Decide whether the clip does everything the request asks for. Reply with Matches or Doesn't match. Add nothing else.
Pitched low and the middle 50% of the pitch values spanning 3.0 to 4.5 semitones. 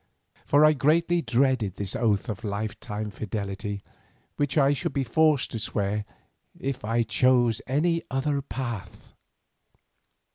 Doesn't match